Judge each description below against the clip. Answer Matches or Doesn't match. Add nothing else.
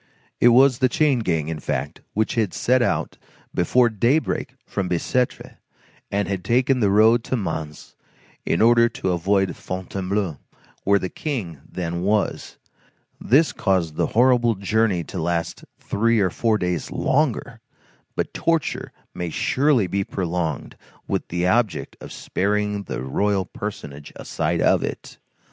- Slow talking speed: Doesn't match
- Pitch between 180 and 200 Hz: Doesn't match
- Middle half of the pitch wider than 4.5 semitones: Matches